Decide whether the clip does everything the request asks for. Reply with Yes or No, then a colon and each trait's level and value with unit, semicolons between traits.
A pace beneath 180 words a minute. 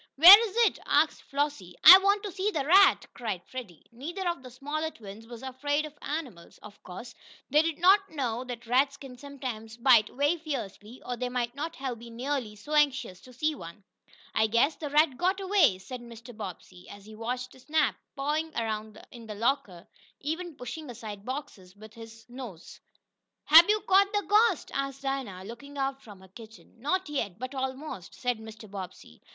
No: average, 185 wpm